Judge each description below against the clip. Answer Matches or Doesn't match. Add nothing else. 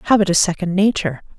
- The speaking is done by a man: Doesn't match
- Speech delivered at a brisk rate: Doesn't match